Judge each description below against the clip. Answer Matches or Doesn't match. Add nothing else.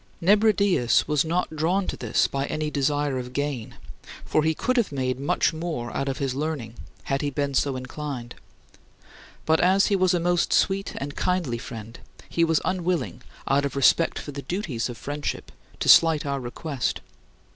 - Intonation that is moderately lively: Matches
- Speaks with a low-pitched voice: Doesn't match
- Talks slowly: Doesn't match